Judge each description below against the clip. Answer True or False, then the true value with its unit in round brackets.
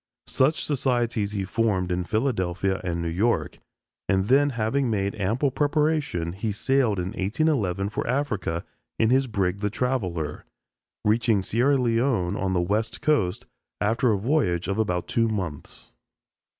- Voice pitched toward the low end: True (110 Hz)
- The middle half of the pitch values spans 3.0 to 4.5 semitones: False (5.1 semitones)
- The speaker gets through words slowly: False (145 wpm)